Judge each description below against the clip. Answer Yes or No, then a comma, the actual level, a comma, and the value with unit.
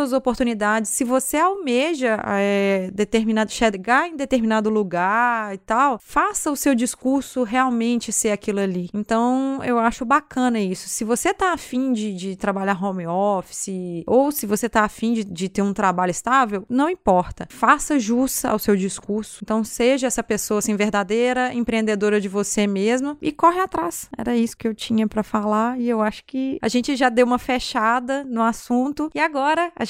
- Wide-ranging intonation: No, average, 3.8 semitones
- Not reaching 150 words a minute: No, average, 175 wpm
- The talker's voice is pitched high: Yes, high, 230 Hz